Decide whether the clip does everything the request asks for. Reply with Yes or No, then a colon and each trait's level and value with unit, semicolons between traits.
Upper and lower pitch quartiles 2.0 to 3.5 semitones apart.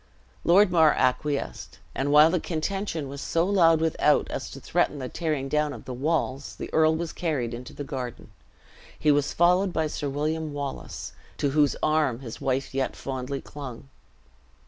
Yes: average, 3.0 semitones